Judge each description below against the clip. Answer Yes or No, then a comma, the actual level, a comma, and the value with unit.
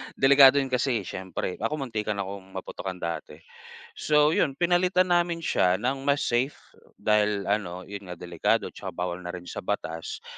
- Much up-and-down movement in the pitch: Yes, wide, 7.3 semitones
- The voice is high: No, low, 105 Hz